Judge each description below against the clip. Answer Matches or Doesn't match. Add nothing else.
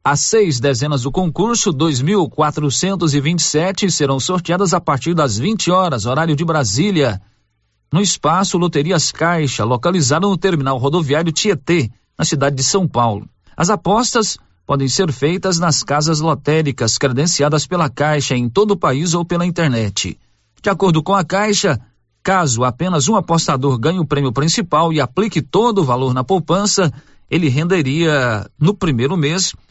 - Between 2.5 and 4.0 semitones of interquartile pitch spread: Doesn't match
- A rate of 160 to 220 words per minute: Doesn't match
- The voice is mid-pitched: Matches